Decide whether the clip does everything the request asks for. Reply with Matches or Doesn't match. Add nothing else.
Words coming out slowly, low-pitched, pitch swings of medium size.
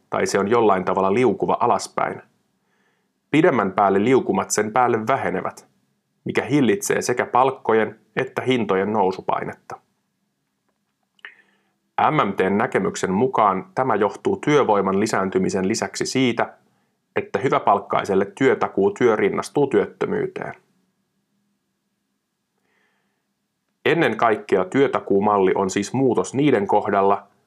Matches